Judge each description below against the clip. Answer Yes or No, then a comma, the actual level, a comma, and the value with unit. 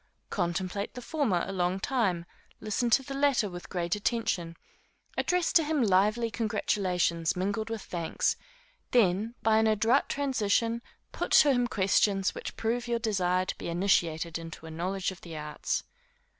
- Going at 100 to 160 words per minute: Yes, average, 155 wpm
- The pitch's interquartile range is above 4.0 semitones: Yes, average, 4.8 semitones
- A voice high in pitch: Yes, high, 200 Hz